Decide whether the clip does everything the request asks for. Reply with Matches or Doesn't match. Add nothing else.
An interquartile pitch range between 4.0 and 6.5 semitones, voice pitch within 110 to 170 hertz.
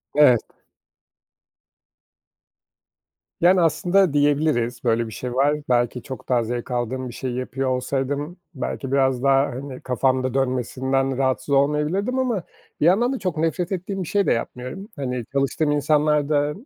Doesn't match